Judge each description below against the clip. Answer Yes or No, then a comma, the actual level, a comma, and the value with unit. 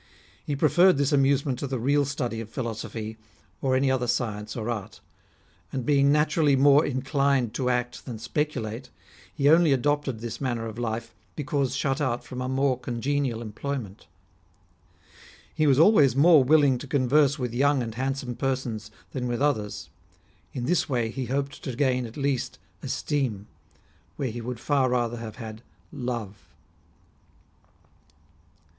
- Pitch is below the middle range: Yes, low, 130 Hz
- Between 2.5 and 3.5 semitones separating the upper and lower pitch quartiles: Yes, average, 3.1 semitones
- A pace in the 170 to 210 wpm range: No, average, 155 wpm